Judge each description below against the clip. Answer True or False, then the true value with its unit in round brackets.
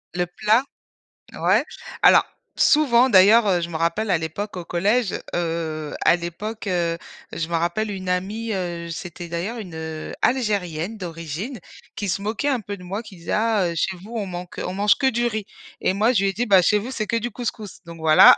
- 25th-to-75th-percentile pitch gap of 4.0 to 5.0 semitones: True (4.3 semitones)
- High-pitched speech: True (195 Hz)